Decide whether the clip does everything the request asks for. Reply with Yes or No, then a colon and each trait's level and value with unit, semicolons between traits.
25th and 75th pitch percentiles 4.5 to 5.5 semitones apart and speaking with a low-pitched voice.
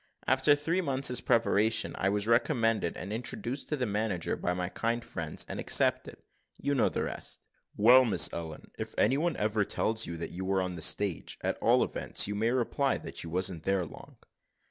Yes: average, 5.2 semitones; low, 110 Hz